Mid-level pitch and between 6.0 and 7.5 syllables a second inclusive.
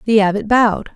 No: high, 215 Hz; 6.2 syllables/s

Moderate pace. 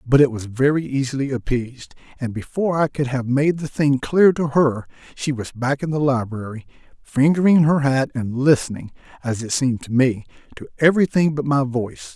Yes: average, 190 wpm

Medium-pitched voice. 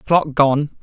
Yes: medium, 145 Hz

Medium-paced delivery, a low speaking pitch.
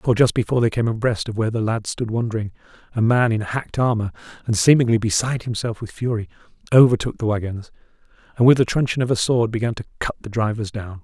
No: fast, 210 wpm; low, 115 Hz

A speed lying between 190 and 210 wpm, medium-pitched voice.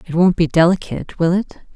Yes: fast, 205 wpm; medium, 175 Hz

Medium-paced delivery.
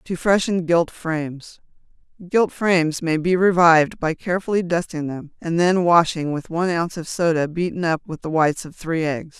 Yes: average, 180 wpm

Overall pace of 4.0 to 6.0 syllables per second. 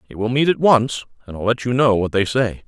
Yes: 5.7 syllables/s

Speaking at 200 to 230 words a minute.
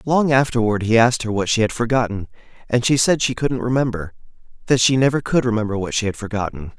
Yes: fast, 205 wpm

